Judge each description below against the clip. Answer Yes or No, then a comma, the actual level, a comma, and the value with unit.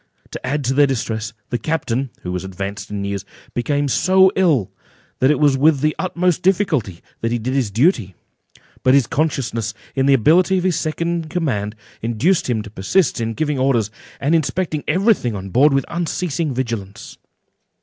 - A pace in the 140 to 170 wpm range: No, average, 180 wpm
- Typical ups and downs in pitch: No, wide, 6.3 semitones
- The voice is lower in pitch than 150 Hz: Yes, low, 135 Hz